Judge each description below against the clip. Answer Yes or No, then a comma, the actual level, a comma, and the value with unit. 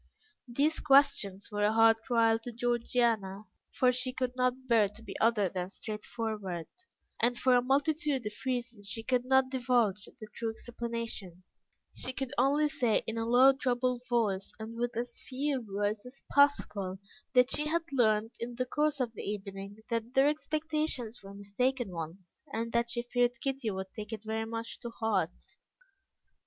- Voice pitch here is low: No, high, 235 Hz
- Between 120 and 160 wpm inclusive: No, average, 170 wpm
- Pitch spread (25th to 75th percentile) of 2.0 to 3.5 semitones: Yes, average, 3.1 semitones